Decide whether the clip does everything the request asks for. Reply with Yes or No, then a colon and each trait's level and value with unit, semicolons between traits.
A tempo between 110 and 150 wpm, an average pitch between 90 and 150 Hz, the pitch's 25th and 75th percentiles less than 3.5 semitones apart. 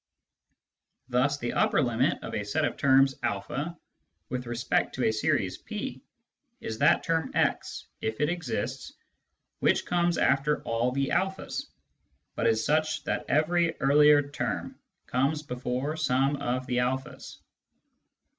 No: average, 145 wpm; medium, 140 Hz; average, 3.8 semitones